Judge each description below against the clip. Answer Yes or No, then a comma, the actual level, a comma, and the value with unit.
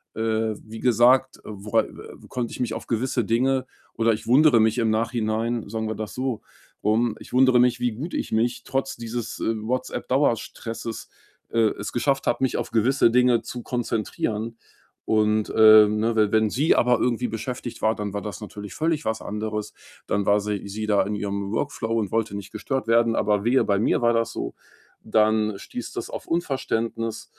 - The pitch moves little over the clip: Yes, narrow, 2.2 semitones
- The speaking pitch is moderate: No, low, 115 Hz